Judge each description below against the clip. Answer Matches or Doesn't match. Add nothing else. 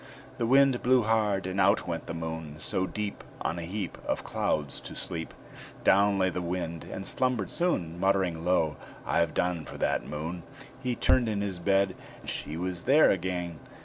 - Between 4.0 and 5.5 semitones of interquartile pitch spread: Doesn't match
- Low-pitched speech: Matches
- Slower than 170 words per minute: Doesn't match